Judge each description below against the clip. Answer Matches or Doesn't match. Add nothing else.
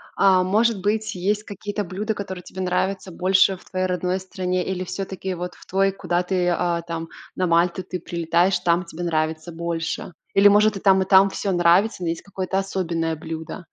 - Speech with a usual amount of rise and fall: Doesn't match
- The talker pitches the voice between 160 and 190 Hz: Matches